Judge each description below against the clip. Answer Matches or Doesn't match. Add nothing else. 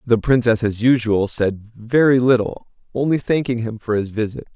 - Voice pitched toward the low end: Matches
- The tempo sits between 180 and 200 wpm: Doesn't match